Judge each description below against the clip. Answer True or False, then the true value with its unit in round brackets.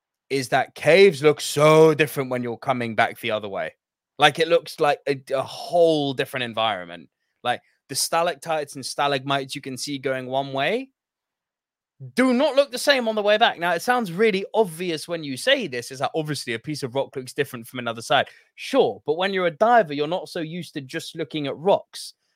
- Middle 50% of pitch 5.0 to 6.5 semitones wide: True (5.3 semitones)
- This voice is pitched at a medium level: True (150 Hz)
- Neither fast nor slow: False (210 wpm)